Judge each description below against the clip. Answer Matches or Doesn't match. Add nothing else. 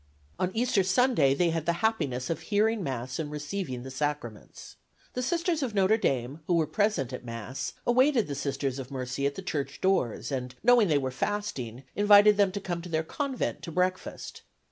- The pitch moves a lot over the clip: Matches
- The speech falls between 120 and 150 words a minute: Doesn't match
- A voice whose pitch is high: Doesn't match